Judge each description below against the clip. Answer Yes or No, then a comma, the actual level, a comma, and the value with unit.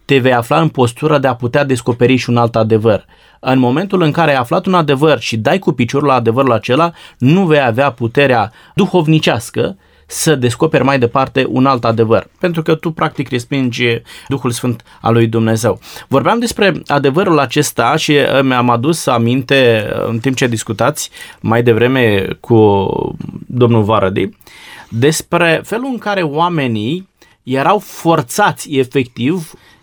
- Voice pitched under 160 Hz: Yes, low, 135 Hz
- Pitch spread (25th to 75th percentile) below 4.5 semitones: No, average, 5.2 semitones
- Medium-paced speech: Yes, average, 150 wpm